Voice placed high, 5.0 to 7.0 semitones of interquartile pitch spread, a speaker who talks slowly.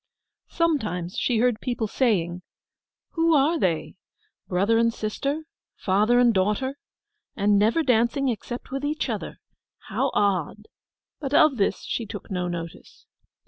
Yes: high, 230 Hz; wide, 5.5 semitones; slow, 120 wpm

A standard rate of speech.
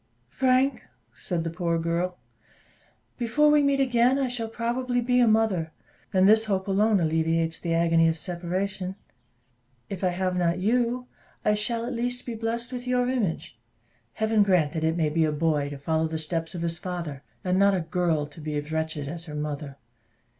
Yes: average, 190 wpm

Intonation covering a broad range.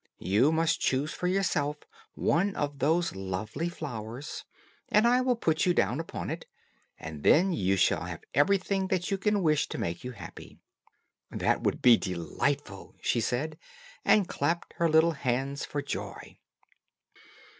Yes: wide, 6.3 semitones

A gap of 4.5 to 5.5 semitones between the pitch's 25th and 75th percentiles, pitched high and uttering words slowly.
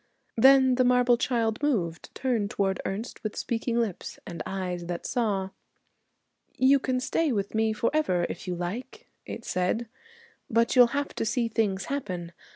No: average, 4.9 semitones; high, 230 Hz; average, 160 wpm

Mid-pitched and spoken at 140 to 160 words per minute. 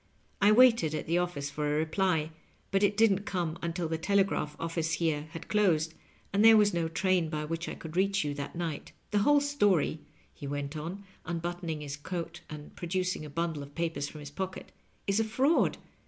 No: medium, 170 Hz; fast, 205 wpm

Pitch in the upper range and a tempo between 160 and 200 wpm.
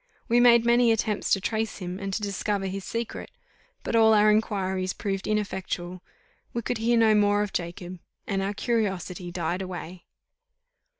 Yes: high, 205 Hz; average, 165 wpm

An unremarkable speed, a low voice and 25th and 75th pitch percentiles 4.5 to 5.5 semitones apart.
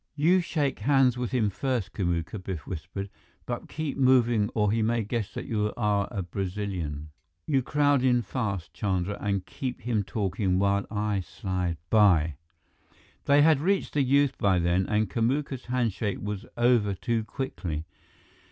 Yes: average, 160 wpm; low, 105 Hz; average, 5.1 semitones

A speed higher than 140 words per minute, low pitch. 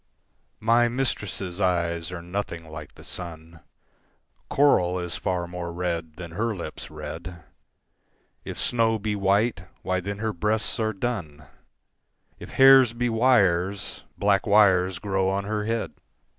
No: slow, 135 wpm; very low, 95 Hz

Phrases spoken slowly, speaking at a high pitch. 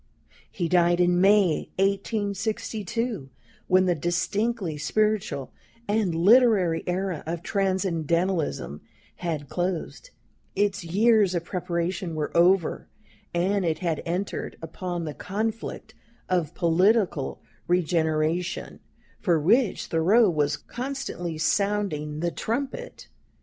No: slow, 100 wpm; medium, 180 Hz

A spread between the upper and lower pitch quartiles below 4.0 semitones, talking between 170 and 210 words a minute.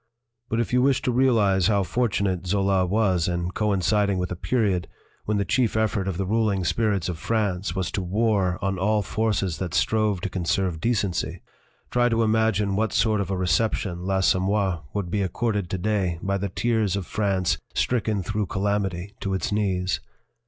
Yes: average, 2.8 semitones; average, 180 wpm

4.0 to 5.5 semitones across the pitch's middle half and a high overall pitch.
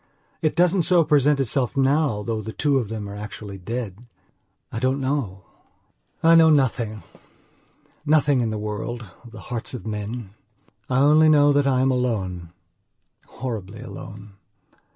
No: average, 5.2 semitones; low, 120 Hz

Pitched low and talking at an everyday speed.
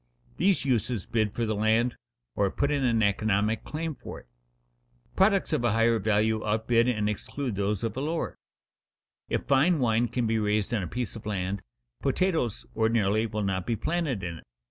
Yes: low, 115 Hz; average, 185 wpm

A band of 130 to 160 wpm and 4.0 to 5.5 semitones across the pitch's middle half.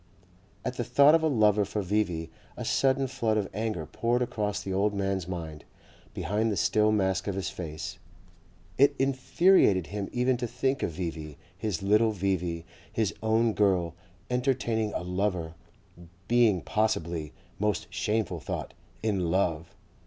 Yes: average, 150 wpm; average, 4.3 semitones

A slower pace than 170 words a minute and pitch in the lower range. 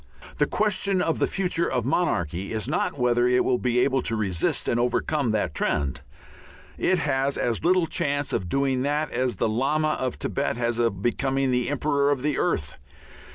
No: average, 180 wpm; low, 130 Hz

